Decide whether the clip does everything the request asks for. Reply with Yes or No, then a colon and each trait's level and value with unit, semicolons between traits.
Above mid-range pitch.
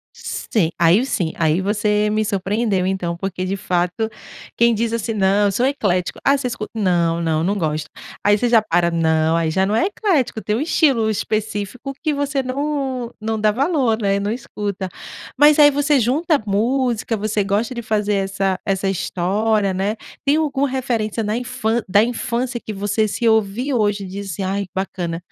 Yes: high, 210 Hz